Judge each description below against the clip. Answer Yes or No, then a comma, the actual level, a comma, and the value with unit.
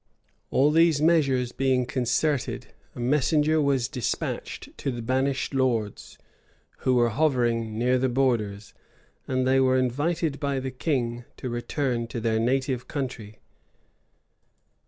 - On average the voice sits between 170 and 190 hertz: No, low, 130 Hz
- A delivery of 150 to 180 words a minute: No, slow, 135 wpm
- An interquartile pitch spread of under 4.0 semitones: Yes, average, 2.7 semitones